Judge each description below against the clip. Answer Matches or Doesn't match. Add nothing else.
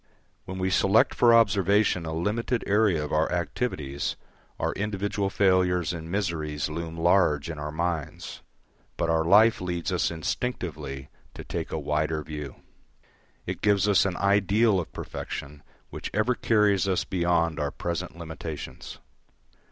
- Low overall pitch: Matches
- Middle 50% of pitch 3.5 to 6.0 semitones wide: Matches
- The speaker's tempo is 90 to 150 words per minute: Matches